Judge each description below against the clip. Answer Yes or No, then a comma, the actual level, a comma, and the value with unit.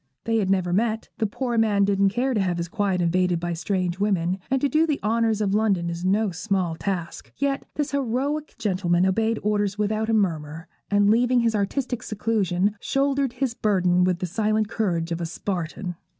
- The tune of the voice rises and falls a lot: No, average, 3.9 semitones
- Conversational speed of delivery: Yes, average, 195 wpm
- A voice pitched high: Yes, high, 205 Hz